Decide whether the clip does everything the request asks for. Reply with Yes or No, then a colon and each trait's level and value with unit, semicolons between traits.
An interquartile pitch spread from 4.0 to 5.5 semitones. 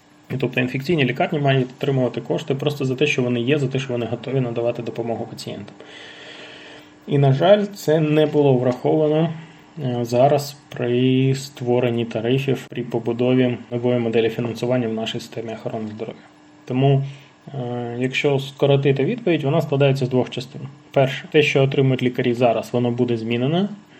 No: average, 3.1 semitones